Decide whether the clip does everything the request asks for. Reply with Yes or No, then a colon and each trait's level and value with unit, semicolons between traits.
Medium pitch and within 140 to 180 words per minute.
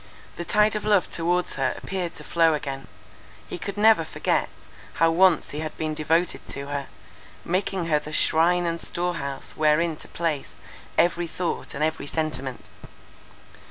Yes: medium, 165 Hz; average, 160 wpm